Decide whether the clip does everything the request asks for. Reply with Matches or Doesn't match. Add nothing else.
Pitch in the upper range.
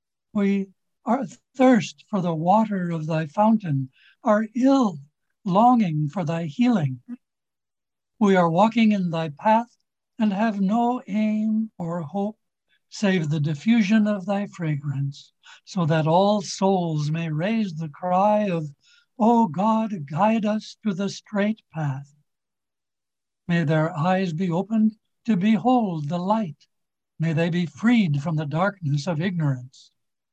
Matches